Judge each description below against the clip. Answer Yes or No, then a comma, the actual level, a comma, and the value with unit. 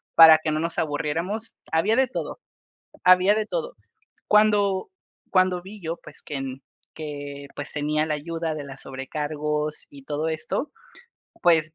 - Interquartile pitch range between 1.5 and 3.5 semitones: No, average, 3.9 semitones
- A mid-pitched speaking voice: Yes, medium, 160 Hz